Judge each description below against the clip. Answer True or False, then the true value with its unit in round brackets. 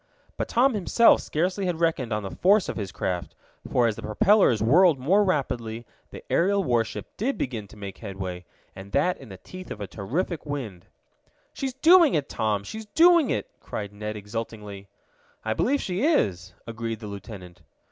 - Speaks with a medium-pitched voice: False (120 Hz)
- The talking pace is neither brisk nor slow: True (175 wpm)